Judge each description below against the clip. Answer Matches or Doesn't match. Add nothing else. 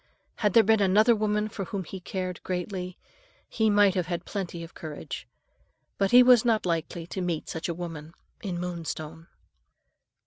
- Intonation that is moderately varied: Matches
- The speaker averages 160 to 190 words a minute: Matches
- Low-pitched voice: Doesn't match